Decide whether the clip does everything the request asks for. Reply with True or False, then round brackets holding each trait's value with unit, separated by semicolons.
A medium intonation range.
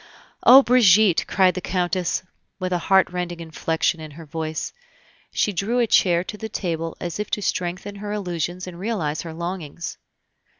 True (3.2 semitones)